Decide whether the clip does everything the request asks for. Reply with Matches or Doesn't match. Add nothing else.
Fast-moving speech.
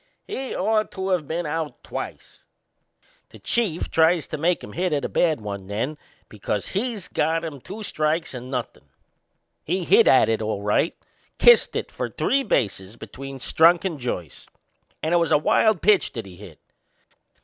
Doesn't match